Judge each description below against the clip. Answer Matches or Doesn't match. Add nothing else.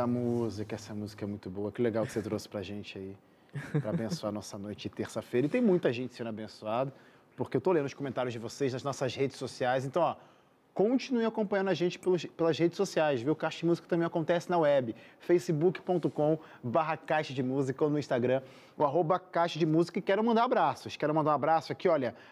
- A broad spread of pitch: Matches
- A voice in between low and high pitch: Matches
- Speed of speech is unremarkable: Doesn't match